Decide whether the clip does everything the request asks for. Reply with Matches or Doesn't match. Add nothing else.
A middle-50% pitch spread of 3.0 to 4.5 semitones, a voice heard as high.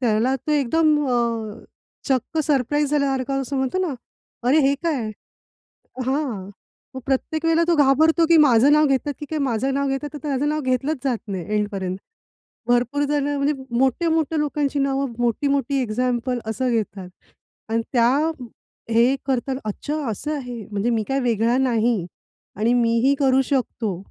Matches